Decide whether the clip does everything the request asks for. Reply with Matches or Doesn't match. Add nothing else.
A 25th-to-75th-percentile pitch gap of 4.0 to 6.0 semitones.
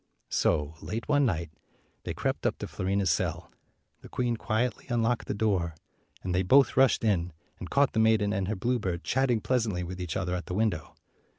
Matches